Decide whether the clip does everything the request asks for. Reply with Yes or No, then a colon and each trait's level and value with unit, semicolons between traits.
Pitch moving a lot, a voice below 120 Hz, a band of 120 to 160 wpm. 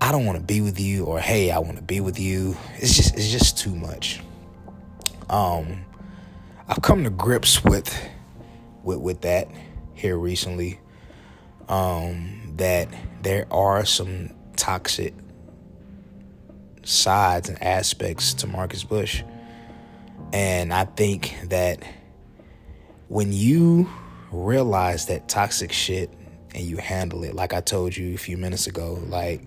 No: average, 2.9 semitones; very low, 90 Hz; slow, 135 wpm